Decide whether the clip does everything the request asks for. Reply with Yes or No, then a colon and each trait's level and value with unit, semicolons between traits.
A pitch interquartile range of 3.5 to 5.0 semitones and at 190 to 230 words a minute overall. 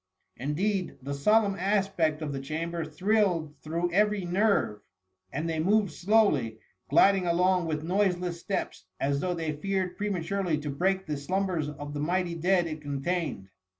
No: average, 4.1 semitones; average, 150 wpm